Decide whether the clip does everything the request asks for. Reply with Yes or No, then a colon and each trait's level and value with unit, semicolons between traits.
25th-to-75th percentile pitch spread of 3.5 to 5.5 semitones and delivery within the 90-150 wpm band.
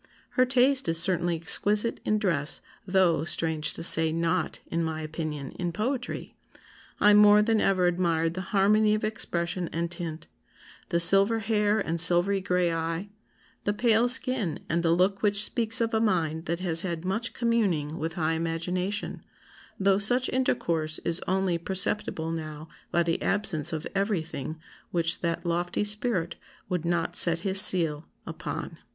No: average, 4.0 semitones; average, 160 wpm